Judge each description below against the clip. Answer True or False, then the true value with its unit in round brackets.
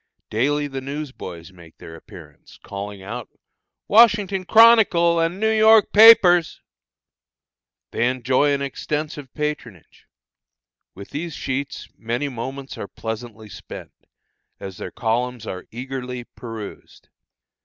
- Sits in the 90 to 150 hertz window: True (135 Hz)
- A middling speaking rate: False (115 wpm)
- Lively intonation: True (6.7 semitones)